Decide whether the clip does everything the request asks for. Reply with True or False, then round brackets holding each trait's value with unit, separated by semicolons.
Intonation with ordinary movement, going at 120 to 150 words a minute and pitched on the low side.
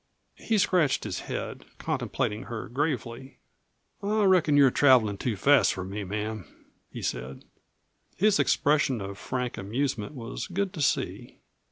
False (6.1 semitones; 140 wpm; 130 Hz)